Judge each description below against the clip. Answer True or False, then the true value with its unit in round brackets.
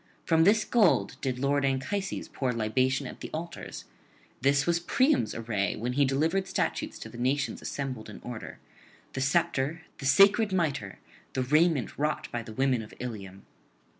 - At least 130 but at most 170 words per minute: True (165 wpm)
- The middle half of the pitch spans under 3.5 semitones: False (5.2 semitones)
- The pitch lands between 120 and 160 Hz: True (135 Hz)